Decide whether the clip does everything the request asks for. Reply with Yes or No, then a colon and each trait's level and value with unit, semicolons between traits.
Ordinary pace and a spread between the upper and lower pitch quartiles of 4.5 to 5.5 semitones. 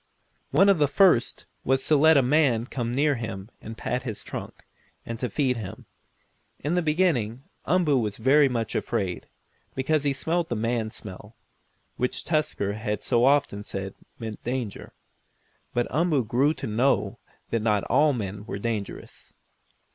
Yes: average, 160 wpm; average, 4.9 semitones